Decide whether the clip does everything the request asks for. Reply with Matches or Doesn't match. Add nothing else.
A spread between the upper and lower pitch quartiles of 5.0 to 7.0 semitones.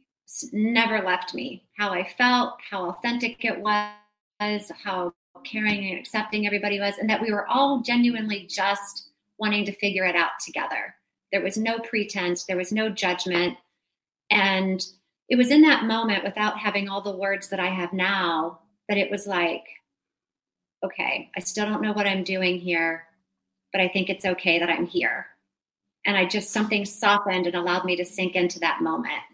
Doesn't match